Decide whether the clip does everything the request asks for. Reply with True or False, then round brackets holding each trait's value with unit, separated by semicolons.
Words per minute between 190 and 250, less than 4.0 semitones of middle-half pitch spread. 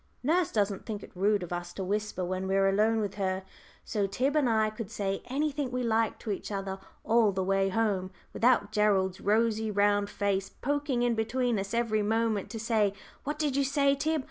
True (205 wpm; 3.5 semitones)